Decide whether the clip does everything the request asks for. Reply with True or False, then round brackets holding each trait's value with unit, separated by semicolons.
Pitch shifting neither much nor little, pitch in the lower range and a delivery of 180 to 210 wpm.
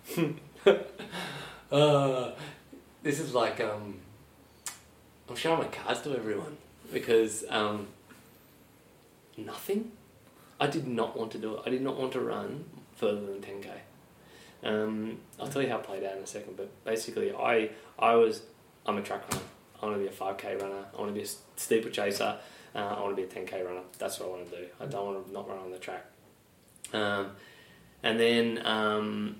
True (4.5 semitones; 110 Hz; 190 wpm)